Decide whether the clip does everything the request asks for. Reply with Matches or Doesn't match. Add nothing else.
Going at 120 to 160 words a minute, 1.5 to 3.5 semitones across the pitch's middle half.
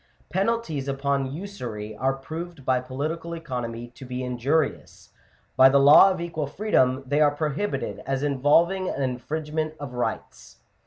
Doesn't match